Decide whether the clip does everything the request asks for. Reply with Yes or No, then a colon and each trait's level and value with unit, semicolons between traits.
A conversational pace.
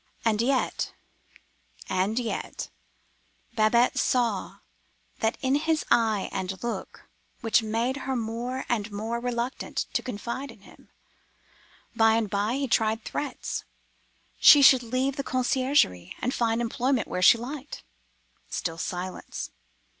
No: slow, 120 wpm